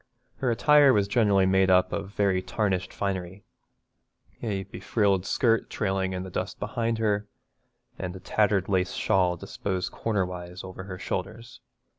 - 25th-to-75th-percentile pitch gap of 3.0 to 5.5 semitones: No, narrow, 2.4 semitones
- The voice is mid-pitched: No, very low, 95 Hz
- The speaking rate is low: No, average, 150 wpm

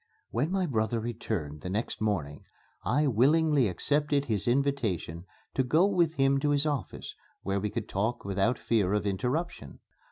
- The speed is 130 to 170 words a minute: Yes, average, 160 wpm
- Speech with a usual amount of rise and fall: No, wide, 6.3 semitones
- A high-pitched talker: No, low, 120 Hz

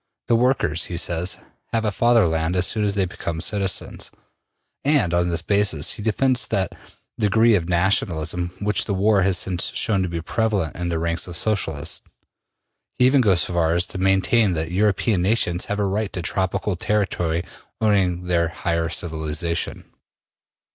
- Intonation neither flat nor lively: Yes, average, 3.6 semitones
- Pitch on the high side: No, very low, 95 Hz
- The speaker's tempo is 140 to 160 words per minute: No, average, 170 wpm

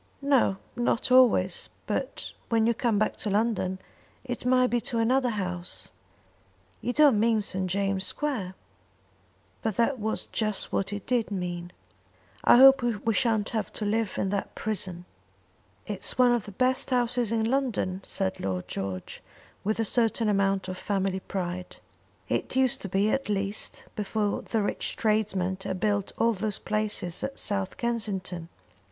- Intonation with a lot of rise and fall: No, average, 3.6 semitones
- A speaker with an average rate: Yes, average, 160 wpm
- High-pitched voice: Yes, high, 215 Hz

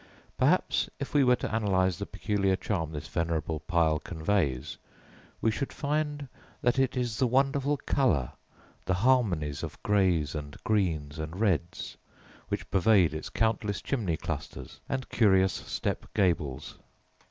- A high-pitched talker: No, very low, 95 Hz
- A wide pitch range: Yes, wide, 7.6 semitones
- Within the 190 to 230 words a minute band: No, average, 140 wpm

